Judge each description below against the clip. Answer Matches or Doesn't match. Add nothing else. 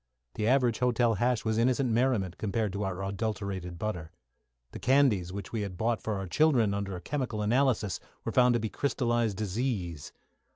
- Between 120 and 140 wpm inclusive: Doesn't match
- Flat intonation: Doesn't match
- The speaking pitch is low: Matches